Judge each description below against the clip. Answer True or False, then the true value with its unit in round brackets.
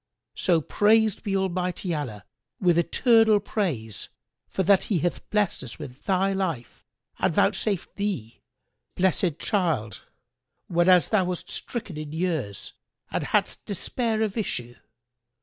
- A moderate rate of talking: False (130 wpm)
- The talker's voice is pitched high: False (180 Hz)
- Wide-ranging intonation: False (4.5 semitones)